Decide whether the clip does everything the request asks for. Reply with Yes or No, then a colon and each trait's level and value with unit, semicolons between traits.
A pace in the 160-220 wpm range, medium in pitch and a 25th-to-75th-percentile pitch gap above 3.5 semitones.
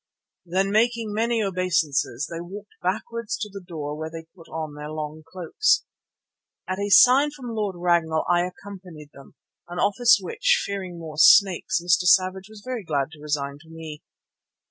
Yes: average, 165 wpm; medium, 180 Hz; average, 4.6 semitones